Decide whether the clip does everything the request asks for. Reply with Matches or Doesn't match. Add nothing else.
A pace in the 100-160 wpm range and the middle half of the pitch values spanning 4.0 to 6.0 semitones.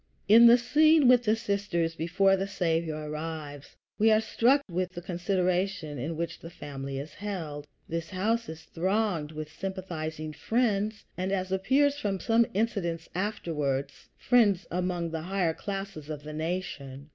Matches